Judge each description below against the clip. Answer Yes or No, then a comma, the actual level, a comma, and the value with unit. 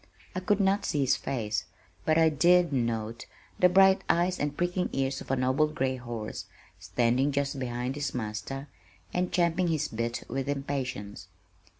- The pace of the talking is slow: No, average, 165 wpm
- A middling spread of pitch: No, wide, 5.8 semitones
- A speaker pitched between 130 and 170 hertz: Yes, low, 135 Hz